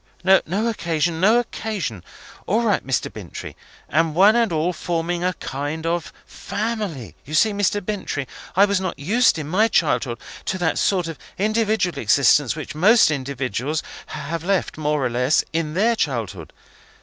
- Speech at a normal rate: Yes, average, 160 wpm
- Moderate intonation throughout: No, wide, 5.7 semitones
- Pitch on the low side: No, medium, 170 Hz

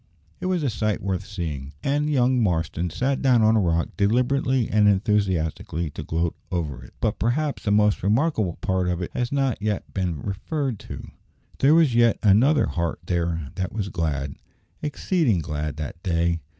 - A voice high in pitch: No, low, 100 Hz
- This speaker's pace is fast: No, average, 175 wpm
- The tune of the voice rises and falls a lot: Yes, wide, 6.6 semitones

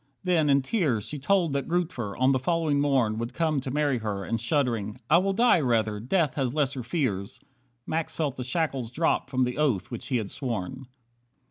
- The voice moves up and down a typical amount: Yes, average, 4.9 semitones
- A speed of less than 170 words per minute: No, average, 200 wpm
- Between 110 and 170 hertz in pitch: Yes, low, 135 Hz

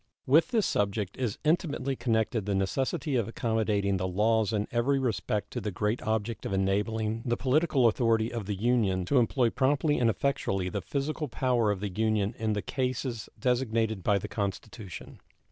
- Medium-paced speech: Yes, average, 175 wpm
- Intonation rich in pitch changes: No, average, 3.7 semitones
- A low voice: Yes, low, 110 Hz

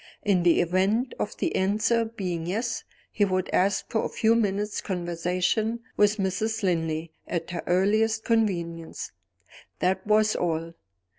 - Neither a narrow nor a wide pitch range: Yes, average, 3.7 semitones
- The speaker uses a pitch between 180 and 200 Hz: Yes, high, 190 Hz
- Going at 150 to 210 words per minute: No, average, 140 wpm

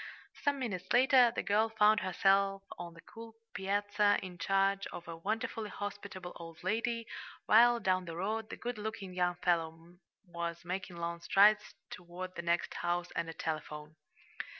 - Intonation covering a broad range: No, average, 3.7 semitones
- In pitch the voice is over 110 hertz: Yes, high, 190 Hz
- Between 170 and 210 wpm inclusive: No, average, 160 wpm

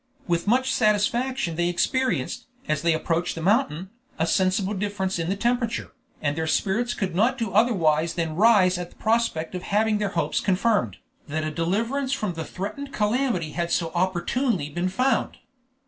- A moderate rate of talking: Yes, average, 170 wpm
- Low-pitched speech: No, high, 190 Hz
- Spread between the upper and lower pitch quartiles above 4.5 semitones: Yes, wide, 5.4 semitones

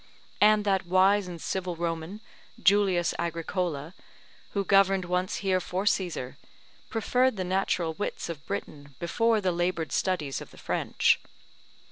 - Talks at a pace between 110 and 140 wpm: Yes, slow, 135 wpm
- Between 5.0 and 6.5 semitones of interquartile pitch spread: No, narrow, 2.6 semitones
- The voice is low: No, medium, 185 Hz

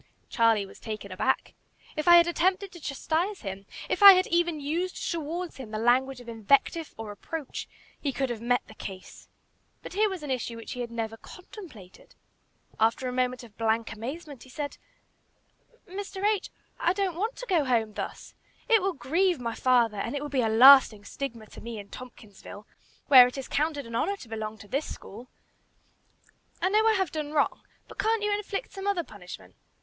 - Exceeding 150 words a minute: Yes, average, 195 wpm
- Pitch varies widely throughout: Yes, wide, 7.4 semitones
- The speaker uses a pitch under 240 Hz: No, very high, 270 Hz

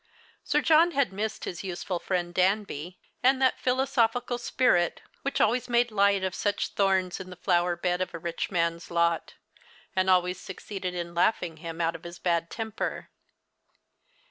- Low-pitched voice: No, medium, 185 Hz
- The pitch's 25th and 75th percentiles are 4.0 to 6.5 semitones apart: Yes, average, 4.4 semitones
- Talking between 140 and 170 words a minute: No, average, 180 wpm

